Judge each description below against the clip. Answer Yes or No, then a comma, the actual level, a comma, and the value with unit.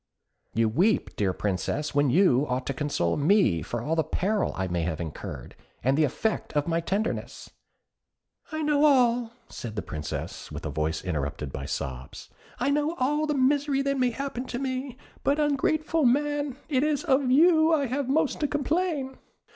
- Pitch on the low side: No, high, 245 Hz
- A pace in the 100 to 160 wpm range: No, average, 180 wpm